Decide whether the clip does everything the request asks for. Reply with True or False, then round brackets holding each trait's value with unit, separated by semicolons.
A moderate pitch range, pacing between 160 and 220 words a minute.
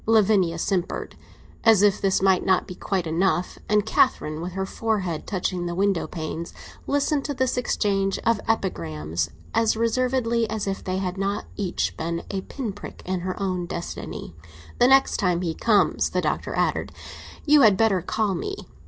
True (3.8 semitones; 170 wpm)